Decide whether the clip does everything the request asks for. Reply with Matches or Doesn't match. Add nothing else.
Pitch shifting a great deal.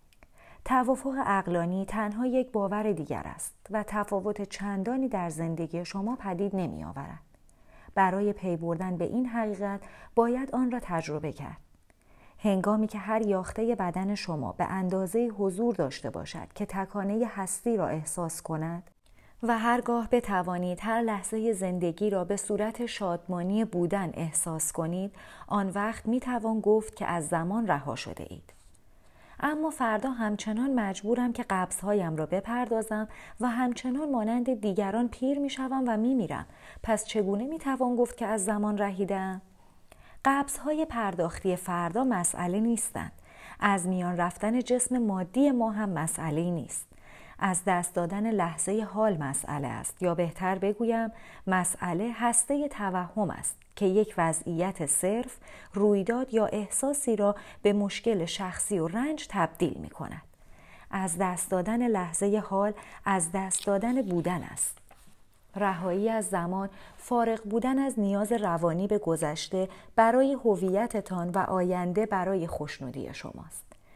Doesn't match